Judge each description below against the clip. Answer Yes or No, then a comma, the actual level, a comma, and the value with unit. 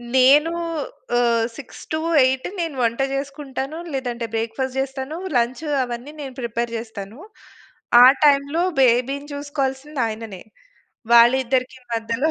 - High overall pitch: Yes, very high, 260 Hz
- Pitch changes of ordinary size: Yes, average, 3.1 semitones